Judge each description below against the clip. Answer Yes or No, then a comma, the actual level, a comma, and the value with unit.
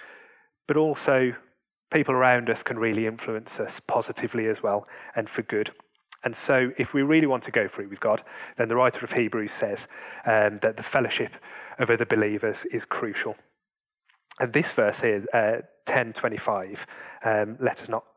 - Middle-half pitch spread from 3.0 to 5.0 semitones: No, wide, 5.5 semitones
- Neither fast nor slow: Yes, average, 170 wpm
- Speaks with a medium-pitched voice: No, low, 125 Hz